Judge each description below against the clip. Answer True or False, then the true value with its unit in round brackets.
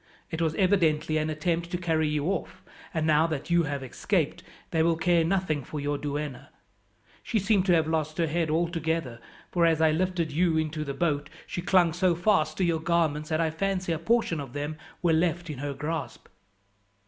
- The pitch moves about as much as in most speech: False (2.2 semitones)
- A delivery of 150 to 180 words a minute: False (200 wpm)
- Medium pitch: True (160 Hz)